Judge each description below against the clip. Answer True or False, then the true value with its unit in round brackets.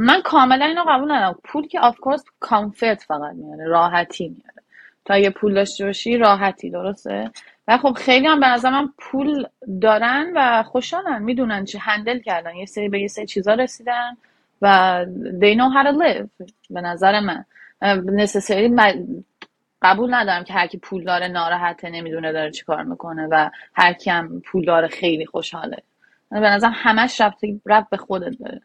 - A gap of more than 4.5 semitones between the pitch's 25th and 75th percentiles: True (5.3 semitones)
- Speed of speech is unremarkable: False (165 wpm)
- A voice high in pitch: True (210 Hz)